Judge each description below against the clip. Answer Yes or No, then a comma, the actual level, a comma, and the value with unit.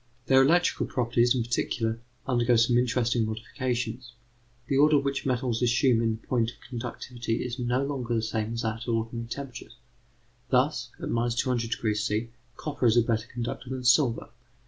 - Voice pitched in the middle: No, low, 120 Hz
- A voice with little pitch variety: Yes, narrow, 1.7 semitones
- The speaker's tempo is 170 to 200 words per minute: No, average, 155 wpm